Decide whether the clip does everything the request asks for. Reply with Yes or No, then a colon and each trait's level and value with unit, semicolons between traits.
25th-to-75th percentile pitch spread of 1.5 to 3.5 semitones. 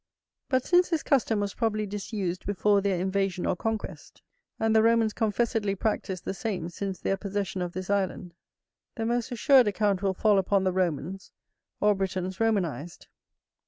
Yes: average, 2.9 semitones